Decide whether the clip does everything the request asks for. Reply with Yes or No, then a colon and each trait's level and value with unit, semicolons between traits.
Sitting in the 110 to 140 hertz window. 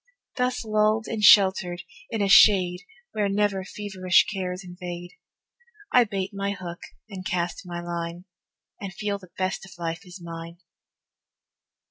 No: high, 190 Hz